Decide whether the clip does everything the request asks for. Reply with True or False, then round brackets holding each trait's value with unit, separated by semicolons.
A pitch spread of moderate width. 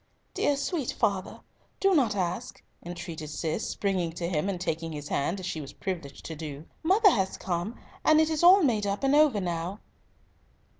False (8.5 semitones)